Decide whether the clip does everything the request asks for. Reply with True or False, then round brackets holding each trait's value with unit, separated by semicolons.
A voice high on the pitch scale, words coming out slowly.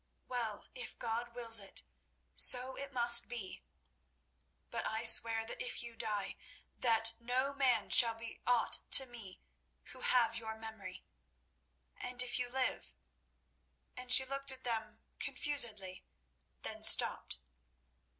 True (235 Hz; 130 wpm)